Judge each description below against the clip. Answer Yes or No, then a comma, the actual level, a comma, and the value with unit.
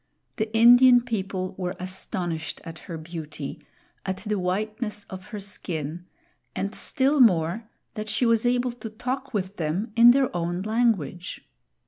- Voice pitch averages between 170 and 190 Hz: No, high, 205 Hz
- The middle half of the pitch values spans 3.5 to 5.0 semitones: Yes, average, 4.7 semitones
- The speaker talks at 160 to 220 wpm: No, average, 145 wpm